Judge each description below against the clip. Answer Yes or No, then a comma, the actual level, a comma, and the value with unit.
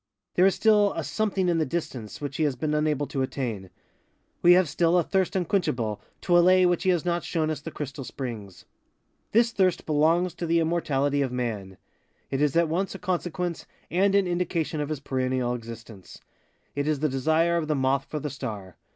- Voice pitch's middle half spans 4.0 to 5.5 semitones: Yes, average, 4.9 semitones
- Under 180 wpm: No, average, 200 wpm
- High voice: No, medium, 155 Hz